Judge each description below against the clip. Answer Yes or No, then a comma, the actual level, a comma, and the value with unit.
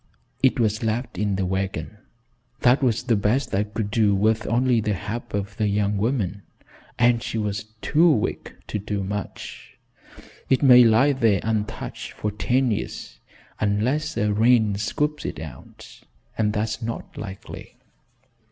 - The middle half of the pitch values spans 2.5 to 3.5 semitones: Yes, average, 2.8 semitones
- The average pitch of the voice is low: Yes, low, 110 Hz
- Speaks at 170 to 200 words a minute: No, average, 150 wpm